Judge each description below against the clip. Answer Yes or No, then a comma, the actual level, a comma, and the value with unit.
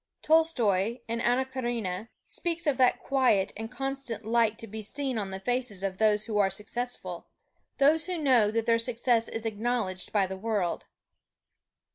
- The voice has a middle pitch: No, high, 230 Hz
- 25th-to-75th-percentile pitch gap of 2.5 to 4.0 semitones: Yes, average, 3.7 semitones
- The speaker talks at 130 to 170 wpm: Yes, average, 165 wpm